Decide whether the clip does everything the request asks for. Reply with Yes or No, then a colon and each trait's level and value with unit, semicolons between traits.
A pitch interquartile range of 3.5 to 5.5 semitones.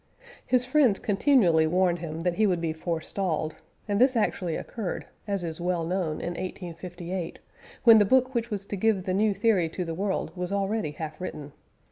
Yes: average, 3.8 semitones